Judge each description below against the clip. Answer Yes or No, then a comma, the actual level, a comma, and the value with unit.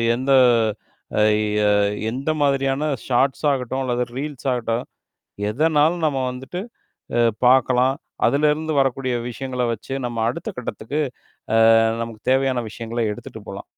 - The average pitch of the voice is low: Yes, low, 130 Hz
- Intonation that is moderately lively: No, narrow, 2.3 semitones